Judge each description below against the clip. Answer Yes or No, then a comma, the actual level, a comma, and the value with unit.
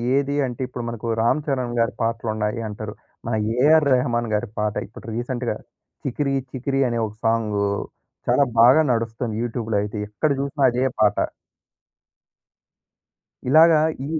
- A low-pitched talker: Yes, low, 120 Hz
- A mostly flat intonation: No, average, 3.5 semitones